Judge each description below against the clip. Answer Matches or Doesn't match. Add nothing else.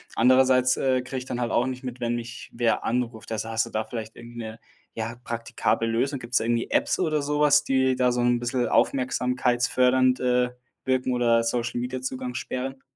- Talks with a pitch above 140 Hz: Doesn't match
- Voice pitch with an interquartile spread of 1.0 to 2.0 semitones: Matches